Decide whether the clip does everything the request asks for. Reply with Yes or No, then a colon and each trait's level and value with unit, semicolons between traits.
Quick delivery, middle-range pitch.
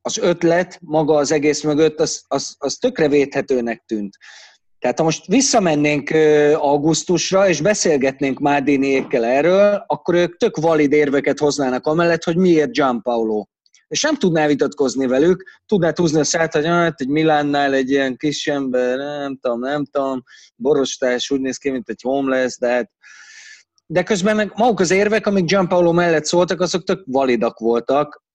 Yes: fast, 165 wpm; medium, 150 Hz